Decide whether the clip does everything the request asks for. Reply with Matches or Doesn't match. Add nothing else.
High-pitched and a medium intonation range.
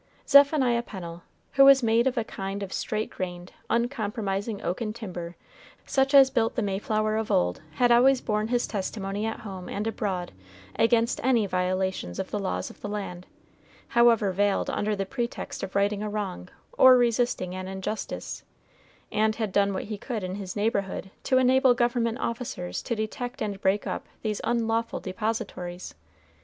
Matches